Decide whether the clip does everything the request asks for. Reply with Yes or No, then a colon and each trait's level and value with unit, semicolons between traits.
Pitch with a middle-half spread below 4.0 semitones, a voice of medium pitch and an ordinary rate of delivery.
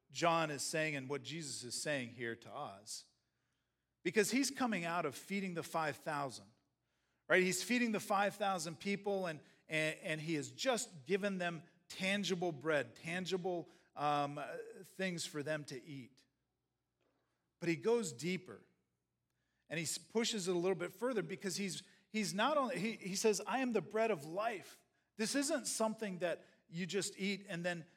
No: average, 4.7 semitones; medium, 180 Hz; average, 165 wpm